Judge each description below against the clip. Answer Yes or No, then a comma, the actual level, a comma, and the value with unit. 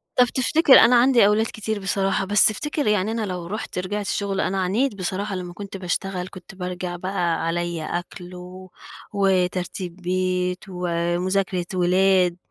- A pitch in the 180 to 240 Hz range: Yes, medium, 185 Hz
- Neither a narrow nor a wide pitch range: No, narrow, 2.2 semitones